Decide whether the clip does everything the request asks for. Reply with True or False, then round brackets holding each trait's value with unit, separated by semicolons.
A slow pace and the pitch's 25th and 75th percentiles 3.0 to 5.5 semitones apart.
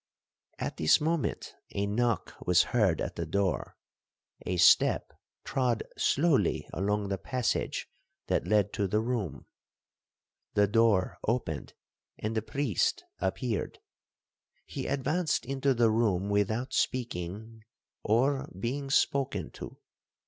True (110 wpm; 4.4 semitones)